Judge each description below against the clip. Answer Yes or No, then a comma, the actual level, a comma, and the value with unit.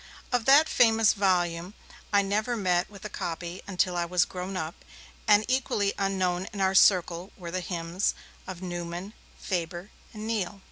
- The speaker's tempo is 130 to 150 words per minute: No, average, 160 wpm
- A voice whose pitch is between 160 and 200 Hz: Yes, high, 190 Hz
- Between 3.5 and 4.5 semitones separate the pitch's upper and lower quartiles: No, average, 2.8 semitones